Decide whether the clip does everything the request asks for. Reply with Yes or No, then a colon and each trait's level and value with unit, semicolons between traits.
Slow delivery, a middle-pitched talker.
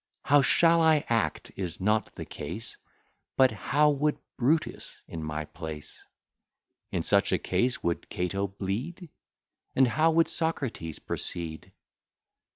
No: slow, 130 wpm; low, 115 Hz